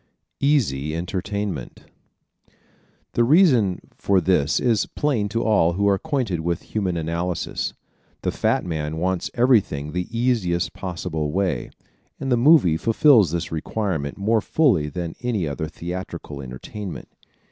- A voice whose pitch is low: Yes, very low, 95 Hz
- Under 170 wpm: Yes, slow, 135 wpm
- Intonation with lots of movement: Yes, wide, 5.7 semitones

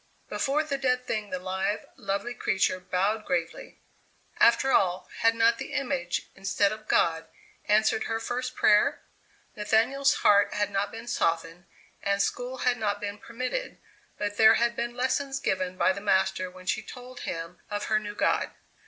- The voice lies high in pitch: Yes, high, 210 Hz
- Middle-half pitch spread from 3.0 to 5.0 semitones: Yes, average, 4.1 semitones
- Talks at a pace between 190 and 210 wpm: No, average, 165 wpm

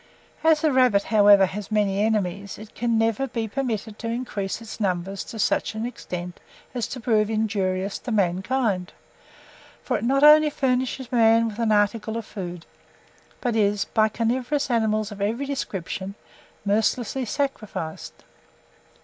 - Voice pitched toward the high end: Yes, high, 220 Hz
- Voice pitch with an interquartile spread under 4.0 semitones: Yes, average, 3.3 semitones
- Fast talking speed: No, average, 150 wpm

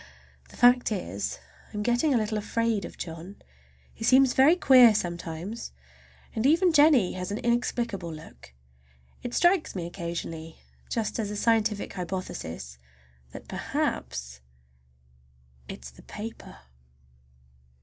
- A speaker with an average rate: No, slow, 130 wpm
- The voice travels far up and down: Yes, wide, 6.0 semitones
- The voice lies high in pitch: Yes, high, 210 Hz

